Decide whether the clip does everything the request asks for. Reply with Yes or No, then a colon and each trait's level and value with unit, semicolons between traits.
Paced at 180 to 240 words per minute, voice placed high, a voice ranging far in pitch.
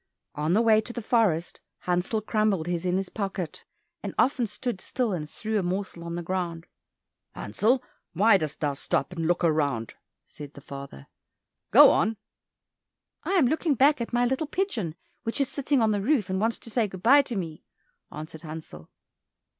Yes: average, 185 wpm; high, 195 Hz; wide, 6.1 semitones